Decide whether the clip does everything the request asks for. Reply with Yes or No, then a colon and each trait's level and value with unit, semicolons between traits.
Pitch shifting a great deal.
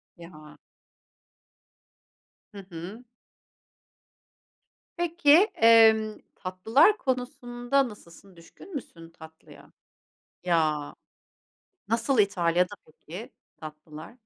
Yes: wide, 6.5 semitones